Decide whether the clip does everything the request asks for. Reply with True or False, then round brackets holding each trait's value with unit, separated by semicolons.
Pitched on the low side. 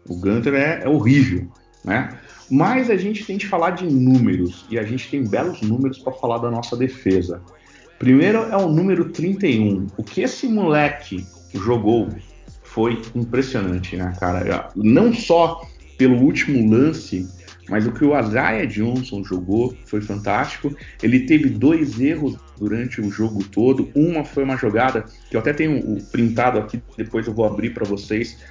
True (115 Hz)